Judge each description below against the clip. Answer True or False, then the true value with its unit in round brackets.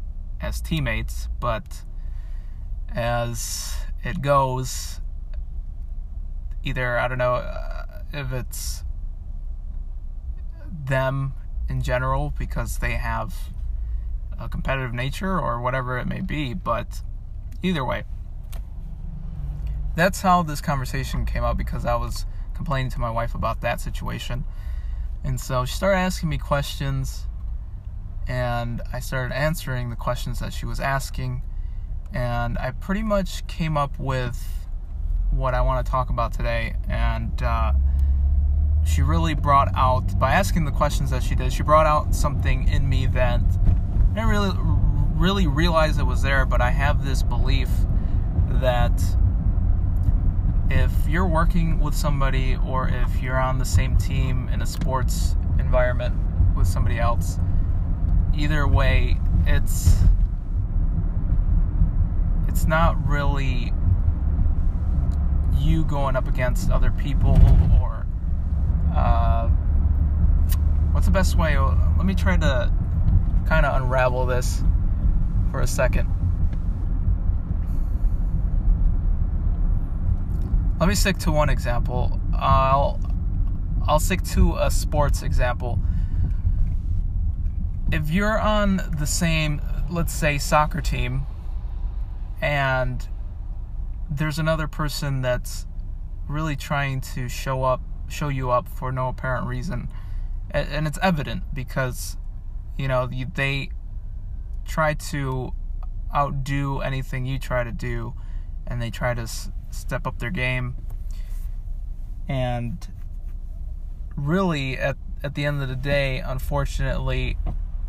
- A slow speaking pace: True (115 wpm)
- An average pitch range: False (7.2 semitones)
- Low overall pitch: True (90 Hz)